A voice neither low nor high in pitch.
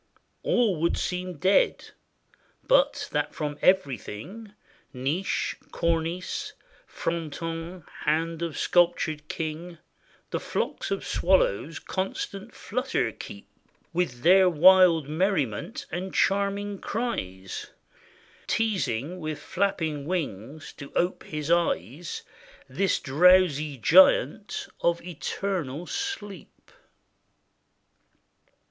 Yes: medium, 170 Hz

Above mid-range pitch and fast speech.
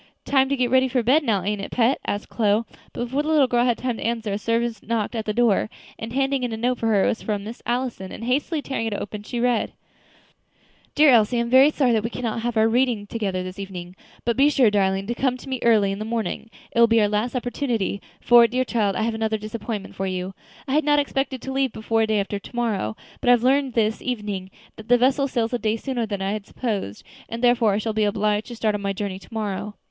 Yes: high, 230 Hz; fast, 260 wpm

